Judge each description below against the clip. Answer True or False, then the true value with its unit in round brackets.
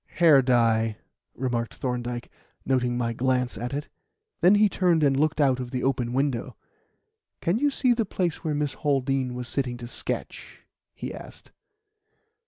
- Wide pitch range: False (3.8 semitones)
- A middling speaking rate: True (160 wpm)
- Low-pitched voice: True (130 Hz)